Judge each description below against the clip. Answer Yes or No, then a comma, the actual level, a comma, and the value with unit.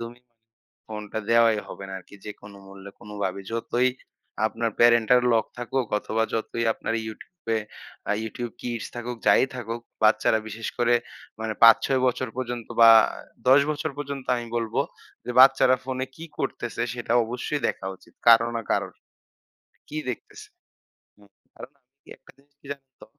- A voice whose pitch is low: Yes, low, 115 Hz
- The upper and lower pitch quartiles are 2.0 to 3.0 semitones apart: Yes, narrow, 2.4 semitones